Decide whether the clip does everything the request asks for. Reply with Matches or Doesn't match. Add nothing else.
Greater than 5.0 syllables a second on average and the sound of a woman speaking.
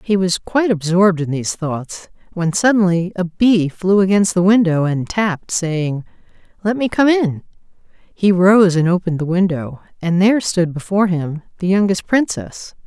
Doesn't match